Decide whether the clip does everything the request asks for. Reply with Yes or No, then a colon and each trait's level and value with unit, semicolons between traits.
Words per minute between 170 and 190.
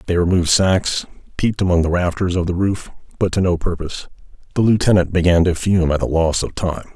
No: fast, 205 wpm